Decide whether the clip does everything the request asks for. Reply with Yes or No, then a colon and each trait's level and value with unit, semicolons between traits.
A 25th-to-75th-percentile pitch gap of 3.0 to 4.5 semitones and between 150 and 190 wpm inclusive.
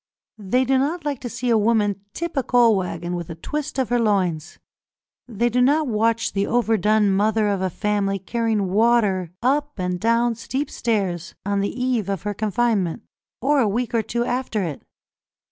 Yes: average, 3.7 semitones; average, 185 wpm